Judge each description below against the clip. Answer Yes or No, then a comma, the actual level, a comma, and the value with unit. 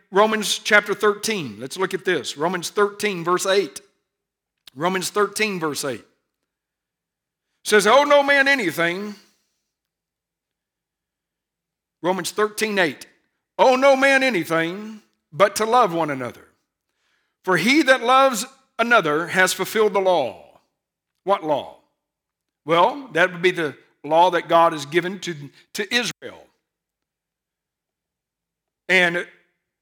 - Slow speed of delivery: Yes, slow, 115 wpm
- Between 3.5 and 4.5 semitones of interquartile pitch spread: Yes, average, 4.1 semitones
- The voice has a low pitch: No, high, 195 Hz